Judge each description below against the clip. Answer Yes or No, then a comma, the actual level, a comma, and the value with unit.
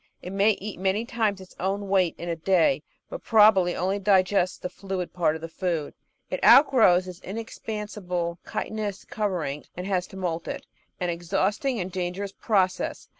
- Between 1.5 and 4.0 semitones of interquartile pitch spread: Yes, narrow, 2.6 semitones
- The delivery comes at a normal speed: Yes, average, 175 wpm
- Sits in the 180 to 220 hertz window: Yes, high, 190 Hz